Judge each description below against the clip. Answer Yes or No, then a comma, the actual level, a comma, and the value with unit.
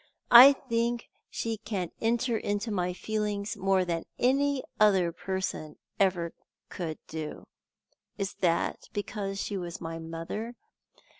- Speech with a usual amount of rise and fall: Yes, average, 4.4 semitones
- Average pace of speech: No, slow, 125 wpm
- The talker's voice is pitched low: No, high, 200 Hz